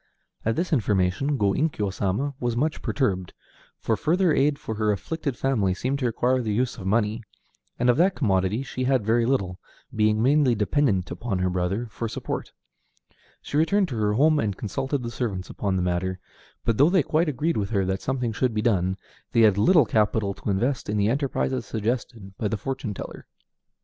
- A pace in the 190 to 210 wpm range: Yes, average, 195 wpm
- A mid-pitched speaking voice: No, low, 115 Hz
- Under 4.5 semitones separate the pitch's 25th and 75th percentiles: No, average, 5.0 semitones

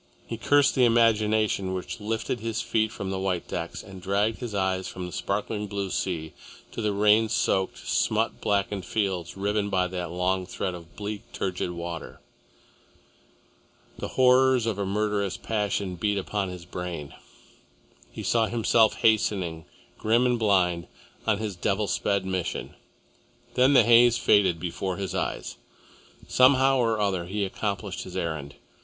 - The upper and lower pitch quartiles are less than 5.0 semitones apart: Yes, average, 3.0 semitones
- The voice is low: Yes, low, 100 Hz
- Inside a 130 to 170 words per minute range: Yes, average, 155 wpm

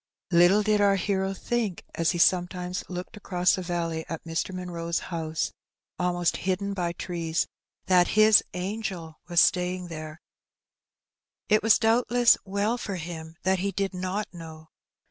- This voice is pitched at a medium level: Yes, medium, 180 Hz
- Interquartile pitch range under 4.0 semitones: Yes, average, 2.8 semitones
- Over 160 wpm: No, average, 150 wpm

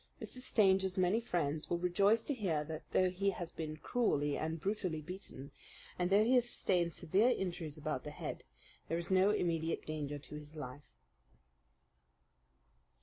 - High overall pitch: No, medium, 175 Hz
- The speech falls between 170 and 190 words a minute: No, average, 160 wpm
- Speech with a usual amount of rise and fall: Yes, average, 4.2 semitones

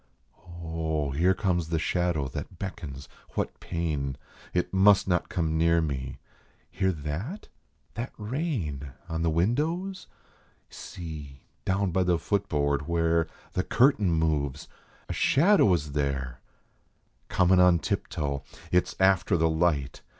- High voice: No, very low, 85 Hz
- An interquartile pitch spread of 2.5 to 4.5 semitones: Yes, average, 4.1 semitones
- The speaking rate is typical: No, slow, 130 wpm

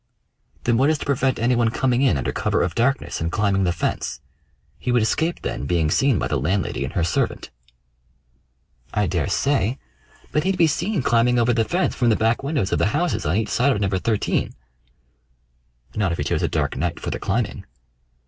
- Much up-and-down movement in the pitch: Yes, wide, 5.9 semitones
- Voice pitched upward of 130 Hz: No, low, 115 Hz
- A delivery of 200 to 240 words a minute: Yes, fast, 205 wpm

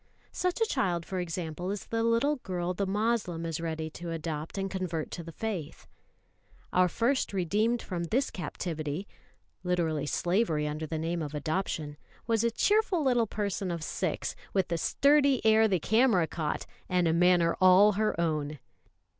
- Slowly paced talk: No, average, 165 wpm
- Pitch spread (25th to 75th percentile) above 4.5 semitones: Yes, average, 5.0 semitones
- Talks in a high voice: No, medium, 180 Hz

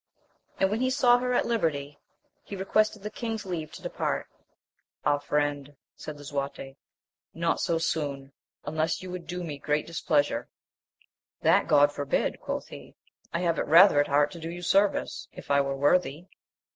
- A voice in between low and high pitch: Yes, medium, 160 Hz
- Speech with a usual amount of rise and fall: Yes, average, 4.5 semitones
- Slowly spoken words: No, average, 170 wpm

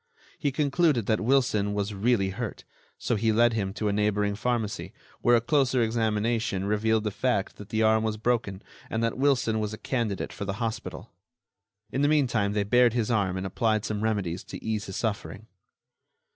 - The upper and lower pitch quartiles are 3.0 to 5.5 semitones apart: No, narrow, 2.6 semitones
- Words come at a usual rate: Yes, average, 185 wpm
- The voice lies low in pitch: Yes, low, 110 Hz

